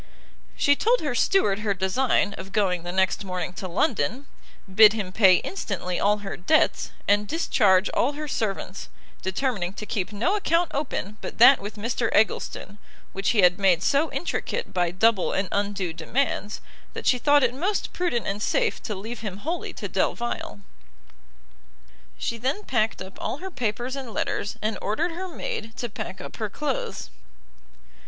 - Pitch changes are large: Yes, wide, 5.7 semitones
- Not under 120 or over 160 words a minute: No, average, 170 wpm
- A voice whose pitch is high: Yes, high, 215 Hz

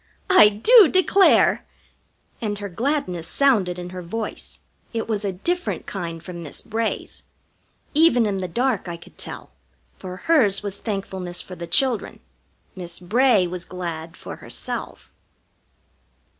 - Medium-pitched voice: No, high, 200 Hz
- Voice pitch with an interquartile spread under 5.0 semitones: No, average, 5.3 semitones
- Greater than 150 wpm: No, average, 140 wpm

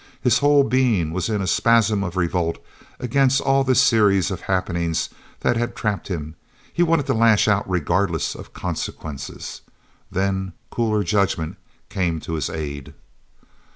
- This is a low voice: Yes, low, 100 Hz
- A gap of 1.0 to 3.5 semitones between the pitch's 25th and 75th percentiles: No, wide, 5.5 semitones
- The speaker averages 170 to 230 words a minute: No, average, 150 wpm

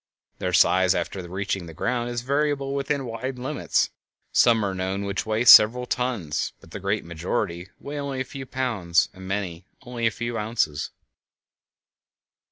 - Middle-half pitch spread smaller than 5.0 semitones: No, average, 5.3 semitones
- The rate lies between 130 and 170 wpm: Yes, average, 160 wpm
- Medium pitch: No, low, 110 Hz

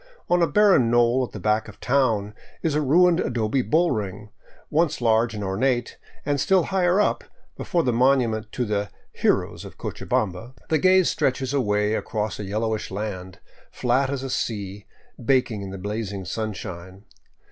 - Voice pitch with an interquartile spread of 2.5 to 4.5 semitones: No, average, 4.9 semitones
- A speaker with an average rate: Yes, average, 175 wpm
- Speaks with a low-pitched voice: Yes, low, 115 Hz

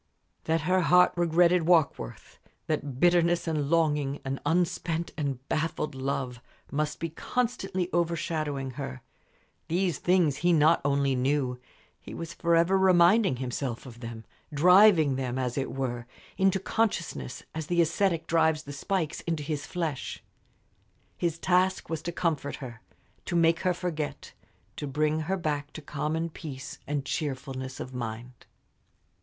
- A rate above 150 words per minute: No, average, 140 wpm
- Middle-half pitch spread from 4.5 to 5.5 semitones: No, average, 4.0 semitones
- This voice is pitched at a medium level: Yes, medium, 155 Hz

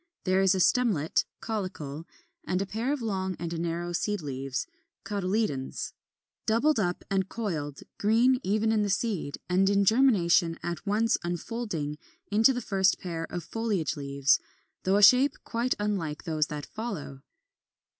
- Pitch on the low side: No, high, 190 Hz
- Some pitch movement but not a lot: Yes, average, 5.0 semitones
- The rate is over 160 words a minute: No, average, 150 wpm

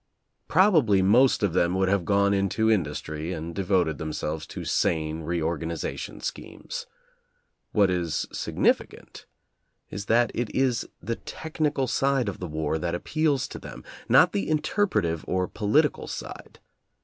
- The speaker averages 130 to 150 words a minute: Yes, average, 145 wpm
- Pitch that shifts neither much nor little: No, wide, 6.6 semitones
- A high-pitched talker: No, very low, 95 Hz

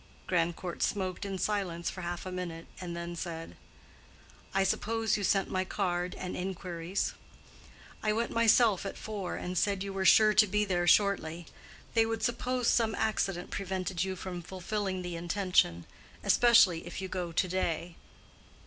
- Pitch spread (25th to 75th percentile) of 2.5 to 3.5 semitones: Yes, average, 2.8 semitones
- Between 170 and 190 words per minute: No, average, 160 wpm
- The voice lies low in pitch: No, medium, 185 Hz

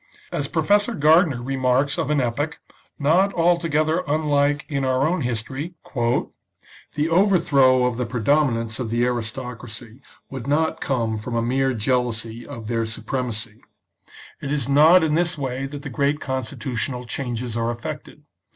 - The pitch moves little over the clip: No, average, 4.0 semitones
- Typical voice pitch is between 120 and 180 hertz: Yes, low, 135 Hz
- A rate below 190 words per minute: Yes, average, 150 wpm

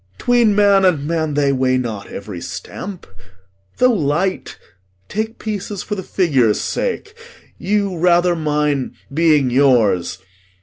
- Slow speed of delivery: Yes, slow, 125 wpm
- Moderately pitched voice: Yes, medium, 165 Hz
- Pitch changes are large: Yes, wide, 6.6 semitones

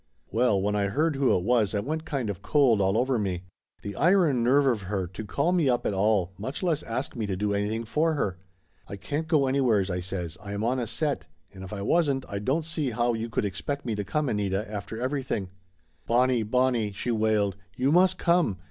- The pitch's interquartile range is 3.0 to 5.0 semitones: No, wide, 5.5 semitones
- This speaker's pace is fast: Yes, fast, 225 wpm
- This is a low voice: Yes, low, 115 Hz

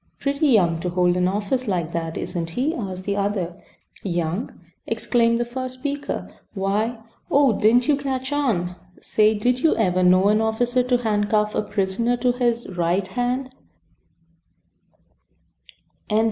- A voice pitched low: No, high, 215 Hz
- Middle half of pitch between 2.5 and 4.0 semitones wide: No, average, 5.2 semitones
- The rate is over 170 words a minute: No, average, 145 wpm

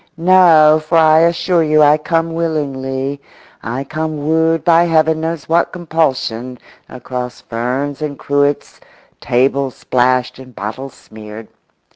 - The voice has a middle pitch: Yes, medium, 150 Hz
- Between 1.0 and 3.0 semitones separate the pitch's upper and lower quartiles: No, average, 3.9 semitones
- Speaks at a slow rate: Yes, slow, 125 wpm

